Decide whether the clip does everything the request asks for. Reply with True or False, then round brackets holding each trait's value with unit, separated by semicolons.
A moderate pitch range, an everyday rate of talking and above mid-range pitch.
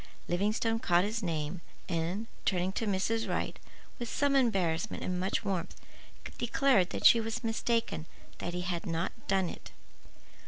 True (4.4 semitones; 150 wpm; 195 Hz)